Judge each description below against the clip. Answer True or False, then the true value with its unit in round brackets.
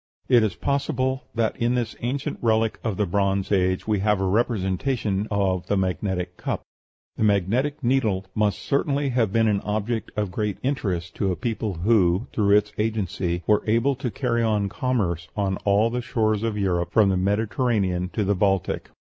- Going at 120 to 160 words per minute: False (180 wpm)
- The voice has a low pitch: True (105 Hz)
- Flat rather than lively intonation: False (3.4 semitones)